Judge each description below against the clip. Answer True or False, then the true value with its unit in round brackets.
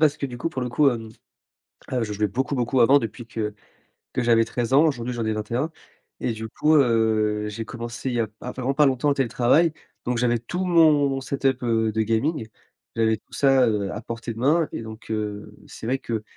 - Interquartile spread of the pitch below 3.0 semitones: False (3.3 semitones)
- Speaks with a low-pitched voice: True (120 Hz)